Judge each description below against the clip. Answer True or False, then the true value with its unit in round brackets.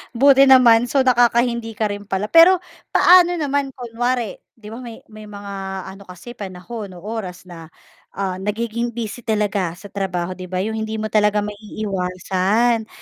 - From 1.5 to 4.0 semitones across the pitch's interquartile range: True (3.7 semitones)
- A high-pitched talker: True (215 Hz)